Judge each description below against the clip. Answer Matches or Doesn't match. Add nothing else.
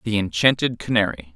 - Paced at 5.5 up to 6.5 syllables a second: Matches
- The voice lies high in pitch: Doesn't match